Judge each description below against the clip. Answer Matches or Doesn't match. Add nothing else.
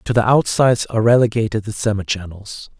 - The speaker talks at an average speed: Matches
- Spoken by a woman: Doesn't match